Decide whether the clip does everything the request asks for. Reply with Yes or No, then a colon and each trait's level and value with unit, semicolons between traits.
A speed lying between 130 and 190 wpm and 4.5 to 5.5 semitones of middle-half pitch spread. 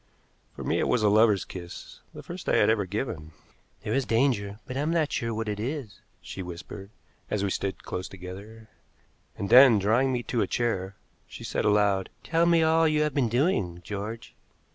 No: average, 200 wpm; average, 4.9 semitones